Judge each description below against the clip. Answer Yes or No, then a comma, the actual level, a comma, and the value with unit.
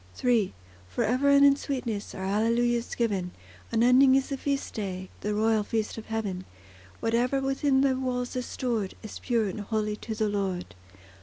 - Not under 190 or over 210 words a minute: No, average, 170 wpm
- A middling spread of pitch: Yes, average, 3.6 semitones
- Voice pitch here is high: Yes, high, 230 Hz